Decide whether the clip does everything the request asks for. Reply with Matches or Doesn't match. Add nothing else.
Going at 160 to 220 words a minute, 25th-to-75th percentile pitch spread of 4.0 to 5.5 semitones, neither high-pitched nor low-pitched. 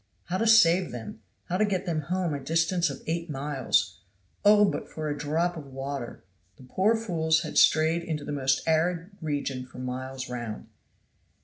Matches